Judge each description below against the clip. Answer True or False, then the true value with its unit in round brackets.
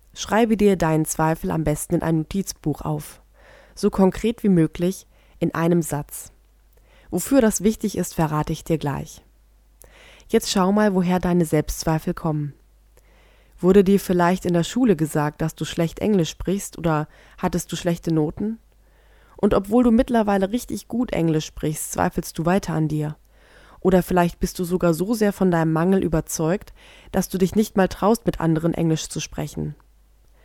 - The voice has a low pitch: False (175 Hz)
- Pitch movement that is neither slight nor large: True (3.6 semitones)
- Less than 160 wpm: False (165 wpm)